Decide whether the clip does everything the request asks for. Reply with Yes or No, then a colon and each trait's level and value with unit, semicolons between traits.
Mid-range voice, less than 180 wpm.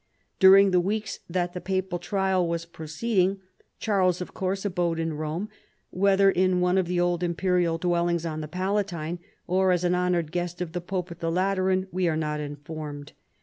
No: medium, 180 Hz; average, 190 wpm